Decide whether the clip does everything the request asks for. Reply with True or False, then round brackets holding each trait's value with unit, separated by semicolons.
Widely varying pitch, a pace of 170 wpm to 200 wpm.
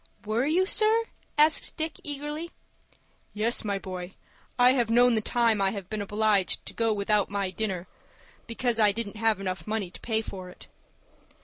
False (3.6 semitones; 175 wpm)